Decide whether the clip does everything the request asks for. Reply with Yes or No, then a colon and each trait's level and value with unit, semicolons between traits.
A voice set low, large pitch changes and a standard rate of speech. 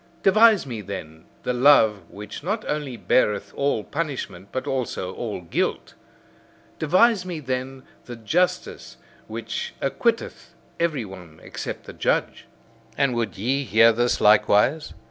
No: low, 125 Hz; wide, 6.0 semitones; slow, 130 wpm